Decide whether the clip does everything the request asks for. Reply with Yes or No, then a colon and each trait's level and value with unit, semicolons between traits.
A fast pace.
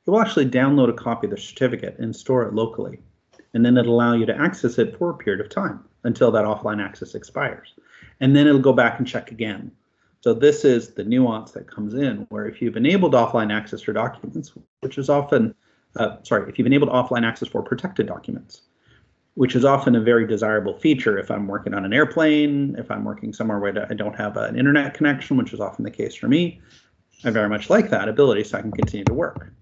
Yes: fast, 225 wpm